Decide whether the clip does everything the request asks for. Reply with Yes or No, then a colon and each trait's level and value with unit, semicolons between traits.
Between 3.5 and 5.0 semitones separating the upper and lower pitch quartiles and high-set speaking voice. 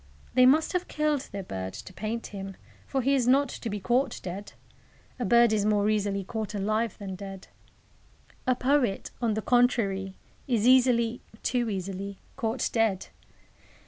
Yes: average, 4.1 semitones; high, 220 Hz